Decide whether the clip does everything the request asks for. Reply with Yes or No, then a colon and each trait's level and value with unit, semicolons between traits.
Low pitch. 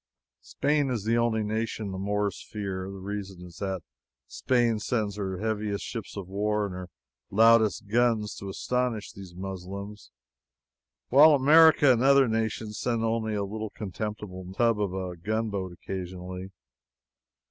Yes: low, 105 Hz